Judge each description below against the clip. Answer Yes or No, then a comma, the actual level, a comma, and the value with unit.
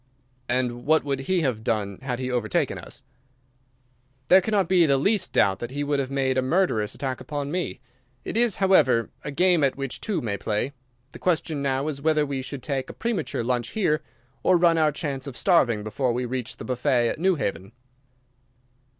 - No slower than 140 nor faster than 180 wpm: No, average, 195 wpm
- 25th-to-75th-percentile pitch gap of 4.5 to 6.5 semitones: Yes, average, 5.0 semitones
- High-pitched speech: No, medium, 140 Hz